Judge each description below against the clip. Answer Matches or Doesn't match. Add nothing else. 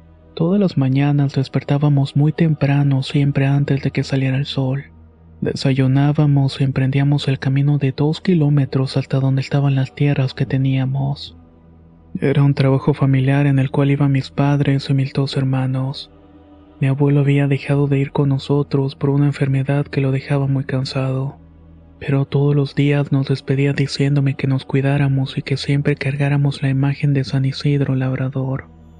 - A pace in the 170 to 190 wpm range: Doesn't match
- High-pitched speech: Doesn't match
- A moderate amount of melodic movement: Doesn't match